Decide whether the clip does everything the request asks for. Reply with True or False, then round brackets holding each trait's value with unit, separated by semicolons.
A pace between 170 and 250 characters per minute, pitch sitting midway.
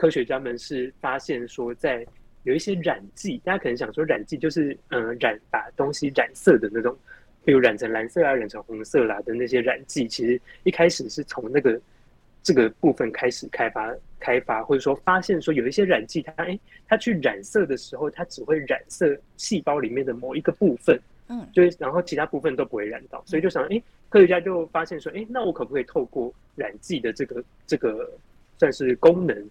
False (315 characters per minute; 160 Hz)